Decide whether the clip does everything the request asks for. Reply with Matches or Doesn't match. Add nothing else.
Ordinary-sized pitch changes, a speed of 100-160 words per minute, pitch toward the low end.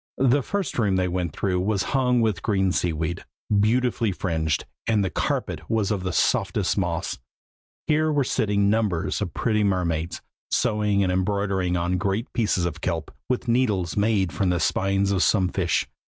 Doesn't match